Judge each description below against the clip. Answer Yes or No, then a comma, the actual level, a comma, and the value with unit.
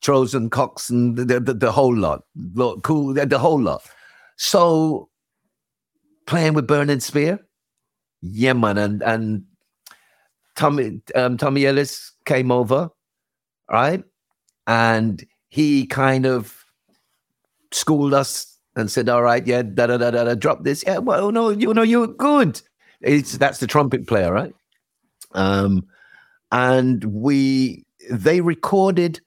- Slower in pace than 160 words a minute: Yes, slow, 135 wpm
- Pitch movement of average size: Yes, average, 4.1 semitones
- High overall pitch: No, low, 135 Hz